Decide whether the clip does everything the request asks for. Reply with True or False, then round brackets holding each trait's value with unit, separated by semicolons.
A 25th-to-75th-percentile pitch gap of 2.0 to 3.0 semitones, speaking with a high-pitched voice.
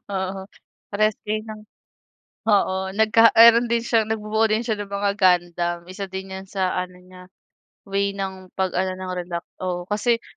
True (2.5 semitones; 195 Hz)